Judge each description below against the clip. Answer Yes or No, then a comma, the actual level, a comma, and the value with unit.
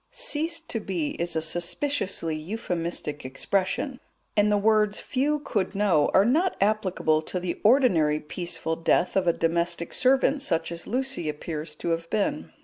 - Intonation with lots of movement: Yes, wide, 6.9 semitones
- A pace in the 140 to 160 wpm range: Yes, average, 155 wpm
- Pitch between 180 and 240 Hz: Yes, medium, 185 Hz